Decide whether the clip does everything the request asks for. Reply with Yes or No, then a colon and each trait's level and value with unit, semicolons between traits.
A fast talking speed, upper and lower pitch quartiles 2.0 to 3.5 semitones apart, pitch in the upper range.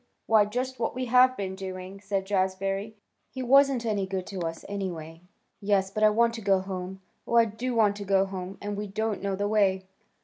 Yes: fast, 210 wpm; average, 2.7 semitones; high, 200 Hz